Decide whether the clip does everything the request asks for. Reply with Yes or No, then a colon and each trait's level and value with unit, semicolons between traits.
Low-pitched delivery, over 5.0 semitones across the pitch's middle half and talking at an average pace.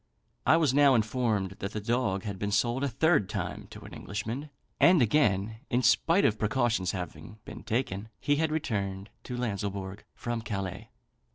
No: low, 110 Hz; average, 4.5 semitones; average, 170 wpm